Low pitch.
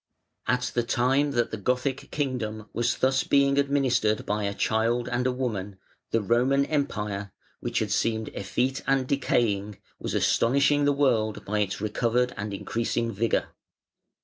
Yes: low, 120 Hz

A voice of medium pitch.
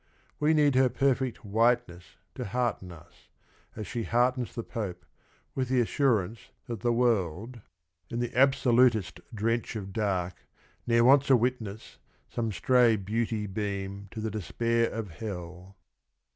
No: low, 115 Hz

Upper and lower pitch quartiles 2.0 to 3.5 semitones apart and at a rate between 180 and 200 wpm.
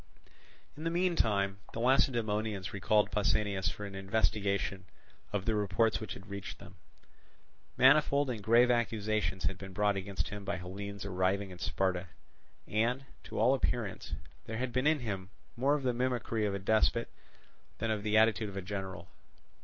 No: average, 3.1 semitones; average, 165 wpm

